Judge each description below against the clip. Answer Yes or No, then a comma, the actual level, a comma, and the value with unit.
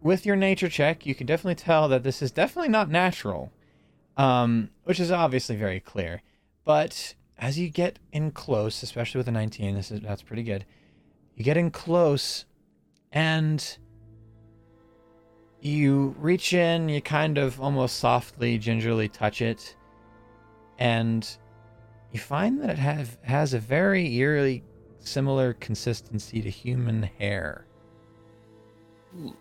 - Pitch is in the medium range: No, low, 125 Hz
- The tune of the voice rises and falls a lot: Yes, wide, 6.0 semitones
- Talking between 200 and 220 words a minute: No, slow, 135 wpm